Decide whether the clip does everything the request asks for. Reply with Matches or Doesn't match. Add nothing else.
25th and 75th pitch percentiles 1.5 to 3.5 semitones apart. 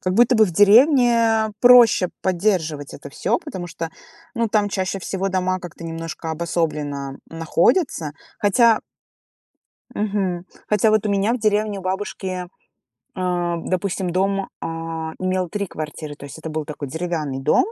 Doesn't match